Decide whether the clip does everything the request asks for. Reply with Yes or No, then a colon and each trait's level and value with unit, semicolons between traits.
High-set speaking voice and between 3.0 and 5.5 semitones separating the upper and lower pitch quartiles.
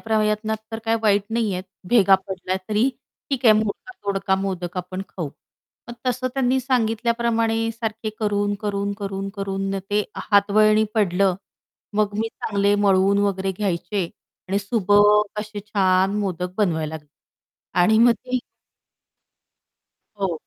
No: high, 205 Hz; narrow, 2.4 semitones